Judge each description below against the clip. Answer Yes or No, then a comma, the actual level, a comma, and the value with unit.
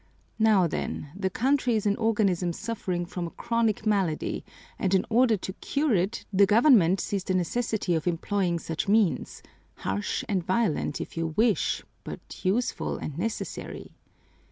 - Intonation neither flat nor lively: Yes, average, 4.2 semitones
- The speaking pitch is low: No, high, 195 Hz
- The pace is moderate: Yes, average, 155 wpm